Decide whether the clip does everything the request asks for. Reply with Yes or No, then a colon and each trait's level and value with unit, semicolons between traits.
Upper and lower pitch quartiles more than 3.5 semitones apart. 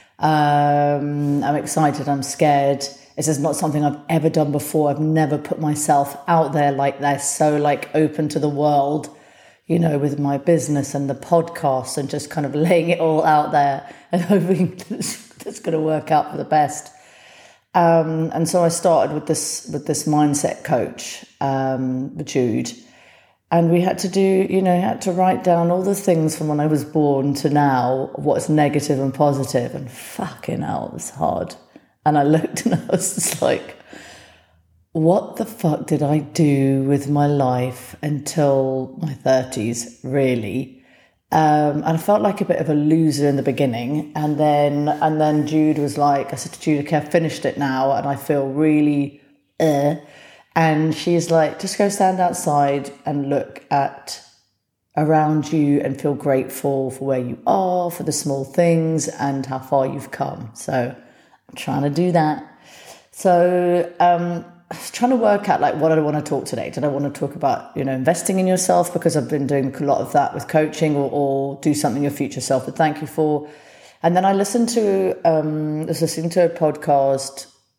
No: narrow, 2.6 semitones